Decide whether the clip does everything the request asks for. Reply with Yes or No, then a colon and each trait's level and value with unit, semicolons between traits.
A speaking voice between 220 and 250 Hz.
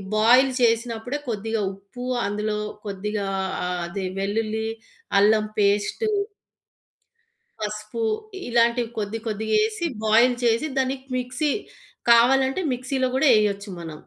Yes: high, 225 Hz